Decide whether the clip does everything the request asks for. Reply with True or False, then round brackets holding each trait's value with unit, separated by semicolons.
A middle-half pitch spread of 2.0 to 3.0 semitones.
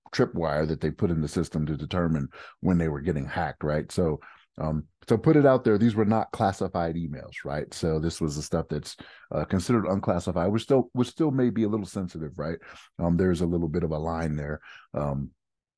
False (5.3 semitones)